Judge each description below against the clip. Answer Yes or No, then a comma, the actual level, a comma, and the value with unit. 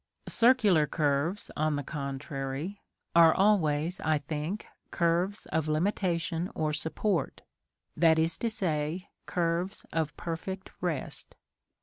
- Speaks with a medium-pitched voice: Yes, medium, 165 Hz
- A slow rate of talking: Yes, slow, 110 wpm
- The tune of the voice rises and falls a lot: No, average, 3.5 semitones